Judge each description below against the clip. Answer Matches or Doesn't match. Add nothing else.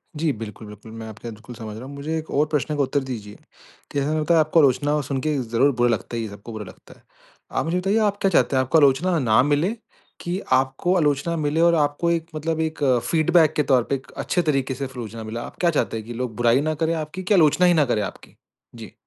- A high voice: Doesn't match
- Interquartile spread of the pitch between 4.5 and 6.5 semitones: Matches